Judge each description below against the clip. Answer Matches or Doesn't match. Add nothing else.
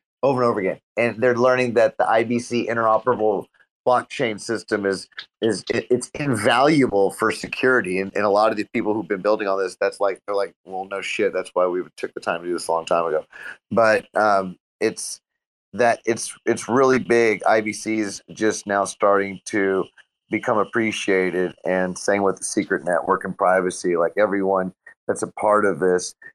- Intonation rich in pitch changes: Doesn't match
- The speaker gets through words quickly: Doesn't match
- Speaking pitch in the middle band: Doesn't match